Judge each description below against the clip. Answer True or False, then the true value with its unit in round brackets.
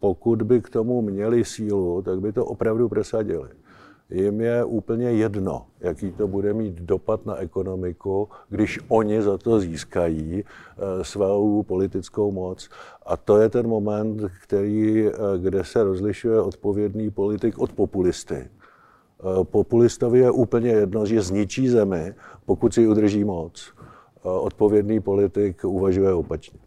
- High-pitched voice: False (105 Hz)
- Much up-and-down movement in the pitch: False (2.4 semitones)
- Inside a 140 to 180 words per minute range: False (130 wpm)